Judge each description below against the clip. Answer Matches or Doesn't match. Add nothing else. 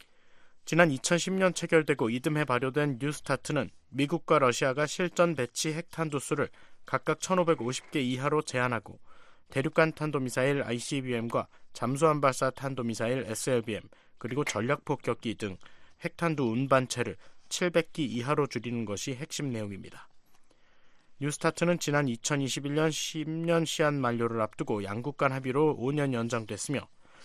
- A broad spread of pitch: Doesn't match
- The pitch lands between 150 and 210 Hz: Doesn't match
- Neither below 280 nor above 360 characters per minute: Matches